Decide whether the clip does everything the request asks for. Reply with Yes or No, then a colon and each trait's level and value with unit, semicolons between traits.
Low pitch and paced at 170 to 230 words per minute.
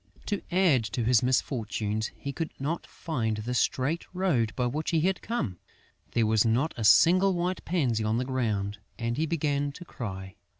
Yes: low, 130 Hz; average, 180 wpm